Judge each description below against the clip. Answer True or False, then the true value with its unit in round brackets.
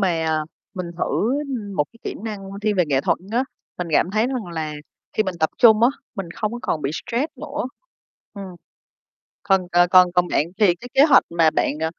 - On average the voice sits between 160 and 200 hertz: True (195 Hz)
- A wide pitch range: False (5.0 semitones)